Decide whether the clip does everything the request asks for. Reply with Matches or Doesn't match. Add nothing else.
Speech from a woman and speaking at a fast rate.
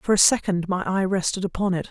Matches